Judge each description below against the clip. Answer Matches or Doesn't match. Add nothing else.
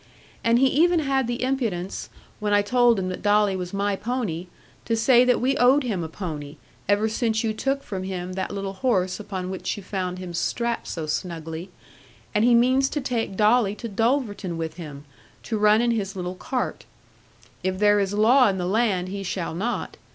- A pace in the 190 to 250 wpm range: Matches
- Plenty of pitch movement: Doesn't match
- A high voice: Matches